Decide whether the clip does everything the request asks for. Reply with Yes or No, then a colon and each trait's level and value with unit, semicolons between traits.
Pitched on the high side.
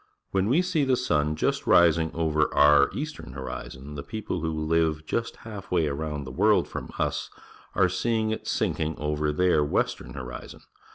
No: very low, 80 Hz